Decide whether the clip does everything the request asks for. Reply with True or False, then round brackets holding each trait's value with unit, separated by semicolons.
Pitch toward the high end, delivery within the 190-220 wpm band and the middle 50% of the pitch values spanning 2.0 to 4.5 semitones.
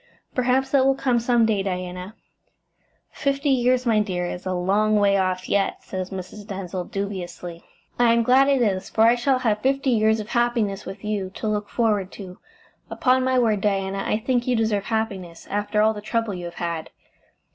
True (210 Hz; 195 wpm; 3.9 semitones)